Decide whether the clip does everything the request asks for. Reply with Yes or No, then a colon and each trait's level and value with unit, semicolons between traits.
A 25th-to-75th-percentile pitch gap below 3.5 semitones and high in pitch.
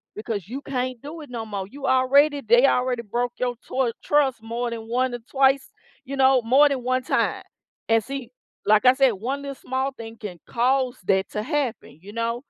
Yes: average, 2.9 semitones; very high, 250 Hz